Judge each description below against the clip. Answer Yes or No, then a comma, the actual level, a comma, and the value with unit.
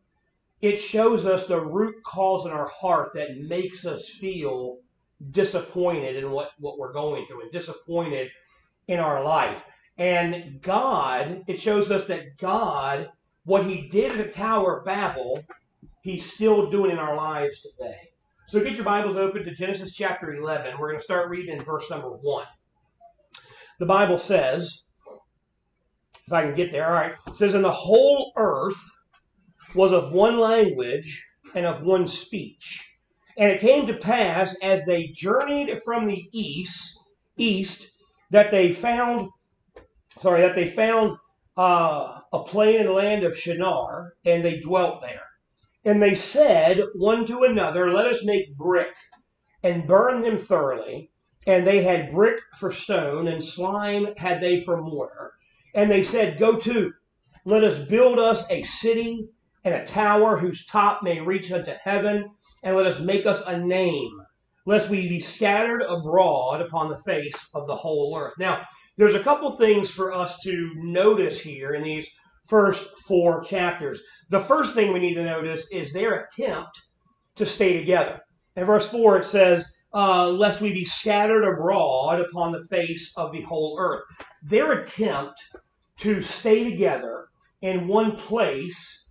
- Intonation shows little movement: No, average, 3.4 semitones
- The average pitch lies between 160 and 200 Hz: Yes, high, 190 Hz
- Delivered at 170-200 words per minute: No, average, 160 wpm